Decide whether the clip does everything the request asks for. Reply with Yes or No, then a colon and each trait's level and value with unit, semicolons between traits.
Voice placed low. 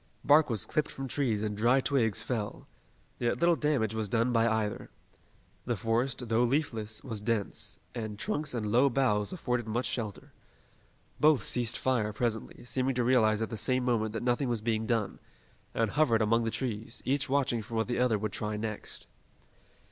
Yes: low, 115 Hz